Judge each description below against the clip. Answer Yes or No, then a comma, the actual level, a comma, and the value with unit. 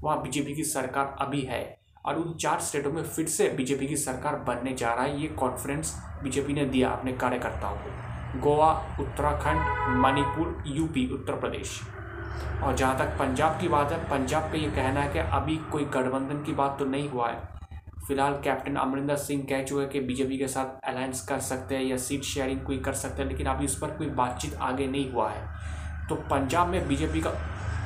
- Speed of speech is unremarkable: No, fast, 200 wpm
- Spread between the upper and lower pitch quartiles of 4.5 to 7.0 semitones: No, average, 2.7 semitones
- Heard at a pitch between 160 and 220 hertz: No, low, 135 Hz